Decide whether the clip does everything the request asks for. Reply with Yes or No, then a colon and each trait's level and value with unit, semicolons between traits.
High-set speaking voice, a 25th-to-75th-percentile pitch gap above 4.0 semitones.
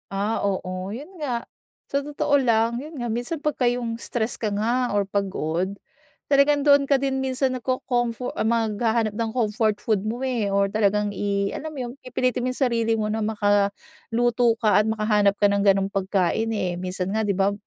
No: high, 220 Hz; average, 3.6 semitones